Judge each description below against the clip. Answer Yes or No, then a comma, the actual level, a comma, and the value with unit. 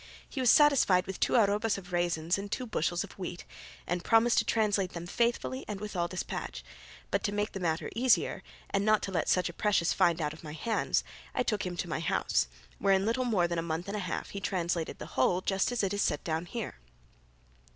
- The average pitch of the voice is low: No, high, 190 Hz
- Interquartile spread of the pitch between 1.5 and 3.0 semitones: No, average, 3.7 semitones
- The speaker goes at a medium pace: No, fast, 230 wpm